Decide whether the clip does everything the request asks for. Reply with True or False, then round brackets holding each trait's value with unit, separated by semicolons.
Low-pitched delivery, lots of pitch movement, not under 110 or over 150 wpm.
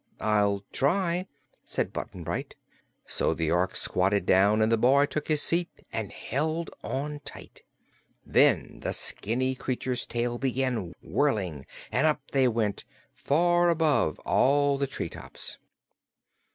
True (130 Hz; 5.8 semitones; 135 wpm)